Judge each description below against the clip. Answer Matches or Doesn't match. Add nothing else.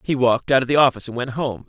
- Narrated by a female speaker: Doesn't match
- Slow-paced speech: Doesn't match